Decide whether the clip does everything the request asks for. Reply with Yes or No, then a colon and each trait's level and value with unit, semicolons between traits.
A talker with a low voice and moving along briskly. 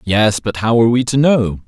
Yes: low, 110 Hz; fast, 250 wpm